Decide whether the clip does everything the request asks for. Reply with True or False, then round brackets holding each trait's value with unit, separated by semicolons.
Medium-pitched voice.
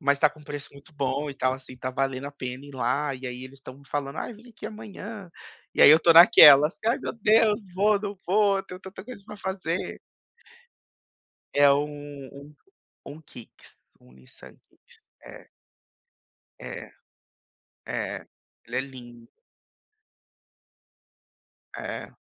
True (145 Hz)